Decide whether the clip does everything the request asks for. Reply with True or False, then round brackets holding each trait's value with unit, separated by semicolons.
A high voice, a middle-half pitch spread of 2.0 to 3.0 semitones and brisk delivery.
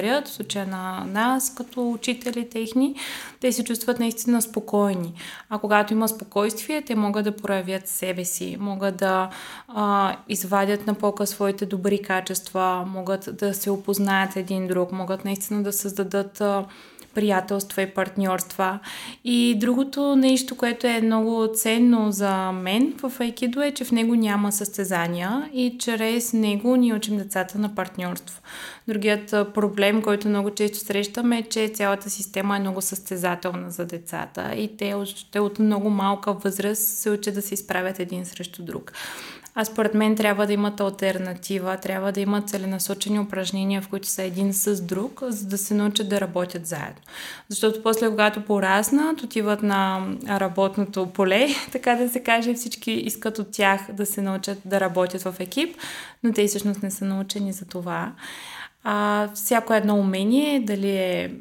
False (205 Hz; 2.4 semitones; 155 wpm)